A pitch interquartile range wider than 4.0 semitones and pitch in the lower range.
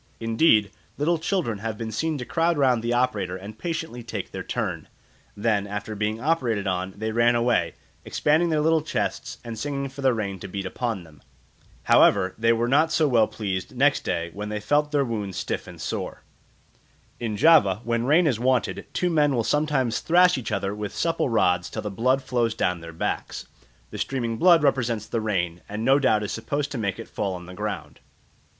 Yes: wide, 5.5 semitones; low, 115 Hz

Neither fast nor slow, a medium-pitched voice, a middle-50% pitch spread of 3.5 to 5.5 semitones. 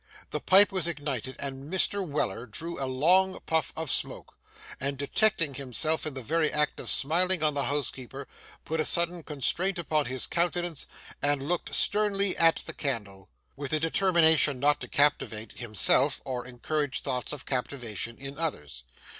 Yes: average, 160 wpm; medium, 145 Hz; average, 4.2 semitones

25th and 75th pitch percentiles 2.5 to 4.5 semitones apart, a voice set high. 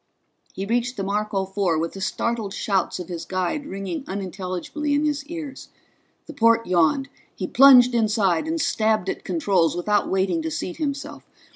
No: average, 5.3 semitones; high, 200 Hz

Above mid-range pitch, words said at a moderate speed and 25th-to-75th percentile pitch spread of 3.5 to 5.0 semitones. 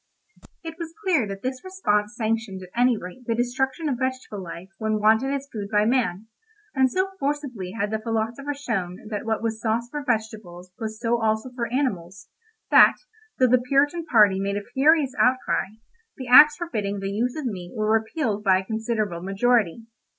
Yes: high, 225 Hz; average, 180 wpm; average, 4.1 semitones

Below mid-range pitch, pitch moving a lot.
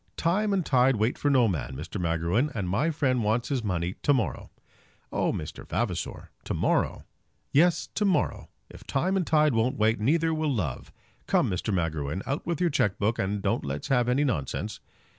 Yes: low, 120 Hz; wide, 7.9 semitones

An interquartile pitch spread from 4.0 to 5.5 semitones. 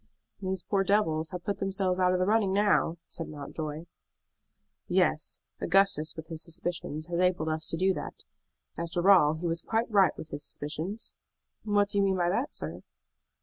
No: average, 3.5 semitones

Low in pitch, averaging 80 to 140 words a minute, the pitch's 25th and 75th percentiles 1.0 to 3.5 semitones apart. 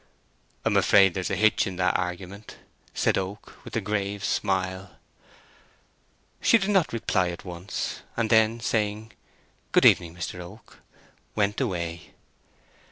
Yes: low, 100 Hz; slow, 135 wpm; average, 3.0 semitones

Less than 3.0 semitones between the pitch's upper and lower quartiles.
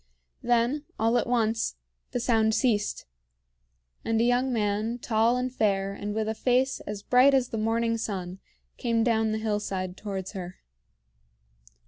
Yes: narrow, 2.6 semitones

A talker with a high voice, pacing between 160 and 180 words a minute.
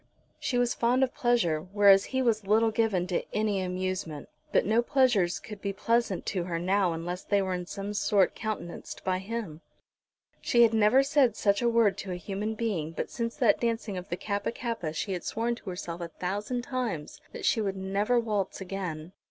No: high, 205 Hz; average, 200 wpm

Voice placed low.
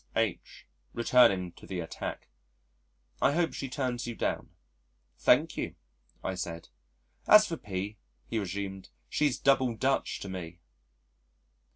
Yes: low, 105 Hz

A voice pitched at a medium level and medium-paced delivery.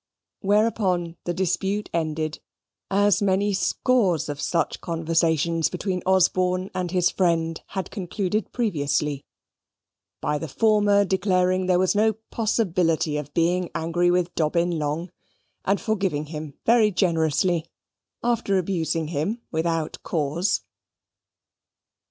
No: medium, 180 Hz; slow, 115 wpm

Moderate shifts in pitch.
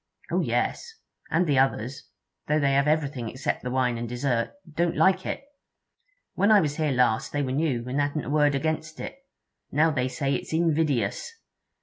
Yes: average, 3.6 semitones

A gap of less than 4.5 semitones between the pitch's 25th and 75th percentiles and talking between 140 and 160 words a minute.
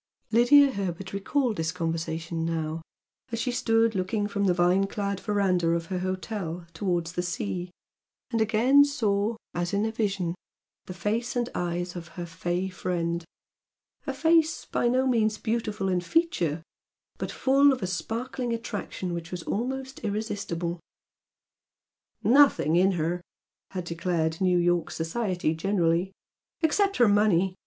No: average, 4.8 semitones; average, 145 wpm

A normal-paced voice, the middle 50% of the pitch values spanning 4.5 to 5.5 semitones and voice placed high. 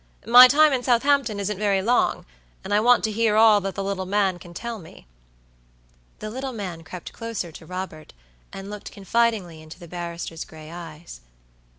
Yes: average, 180 wpm; average, 4.8 semitones; high, 200 Hz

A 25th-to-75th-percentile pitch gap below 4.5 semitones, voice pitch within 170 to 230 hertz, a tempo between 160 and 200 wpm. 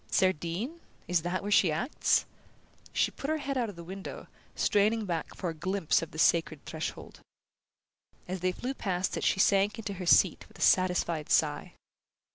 Yes: average, 3.4 semitones; medium, 185 Hz; average, 180 wpm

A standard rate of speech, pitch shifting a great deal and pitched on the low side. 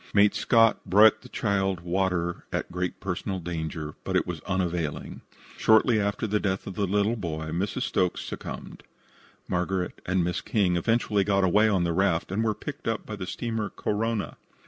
No: average, 175 wpm; average, 3.2 semitones; very low, 95 Hz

